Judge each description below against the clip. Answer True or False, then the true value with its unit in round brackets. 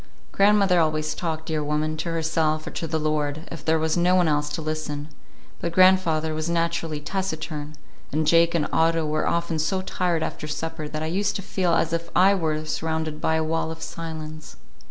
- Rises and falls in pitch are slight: True (1.5 semitones)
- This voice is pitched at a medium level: True (160 Hz)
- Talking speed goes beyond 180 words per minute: True (195 wpm)